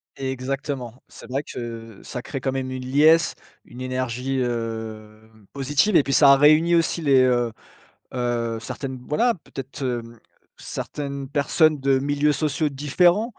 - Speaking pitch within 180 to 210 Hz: No, low, 135 Hz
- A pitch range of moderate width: Yes, average, 3.2 semitones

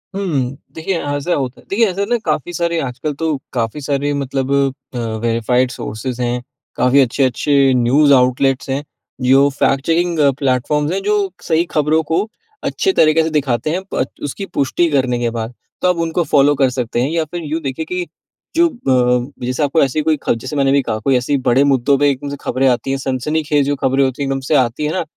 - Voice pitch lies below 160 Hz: Yes, medium, 140 Hz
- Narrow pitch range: No, average, 3.6 semitones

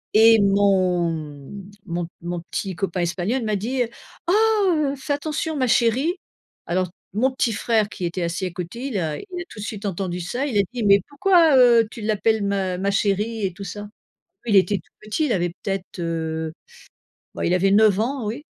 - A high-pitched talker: Yes, high, 205 Hz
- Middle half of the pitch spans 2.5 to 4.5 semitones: No, average, 4.9 semitones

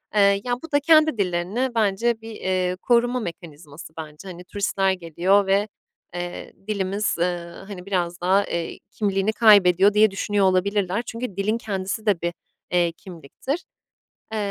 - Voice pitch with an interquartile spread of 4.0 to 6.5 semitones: No, average, 3.3 semitones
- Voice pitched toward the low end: No, high, 195 Hz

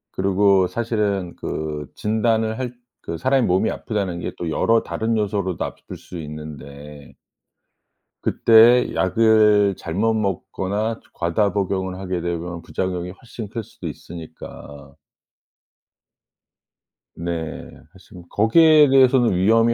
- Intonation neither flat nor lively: Yes, average, 4.5 semitones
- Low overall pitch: Yes, low, 100 Hz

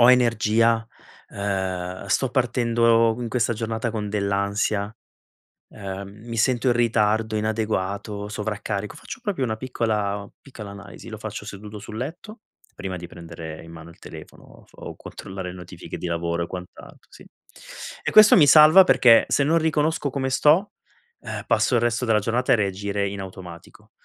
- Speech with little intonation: No, average, 3.3 semitones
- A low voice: Yes, low, 110 Hz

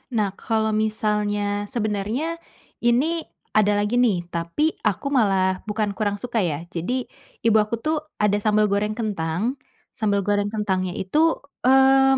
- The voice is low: No, high, 210 Hz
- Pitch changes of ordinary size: No, narrow, 2.0 semitones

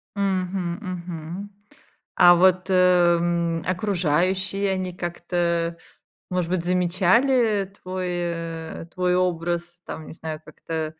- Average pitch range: No, narrow, 1.5 semitones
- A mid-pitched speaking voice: Yes, medium, 175 Hz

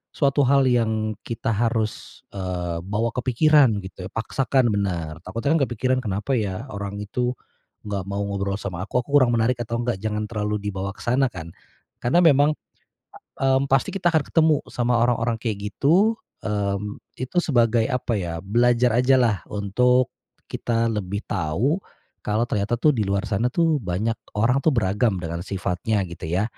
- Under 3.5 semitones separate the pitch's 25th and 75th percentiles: No, average, 4.0 semitones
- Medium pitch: No, low, 115 Hz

